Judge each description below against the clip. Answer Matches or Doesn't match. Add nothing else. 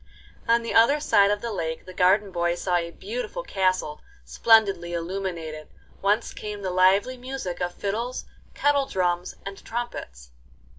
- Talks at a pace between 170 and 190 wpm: Doesn't match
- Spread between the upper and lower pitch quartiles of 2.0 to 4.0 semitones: Doesn't match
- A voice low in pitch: Doesn't match